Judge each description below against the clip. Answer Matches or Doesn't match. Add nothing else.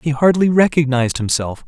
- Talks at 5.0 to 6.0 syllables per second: Matches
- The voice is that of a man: Matches